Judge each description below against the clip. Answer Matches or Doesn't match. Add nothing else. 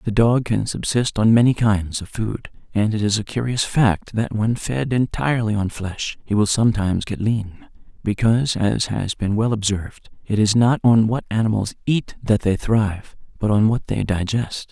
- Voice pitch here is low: Matches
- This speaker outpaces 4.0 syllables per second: Matches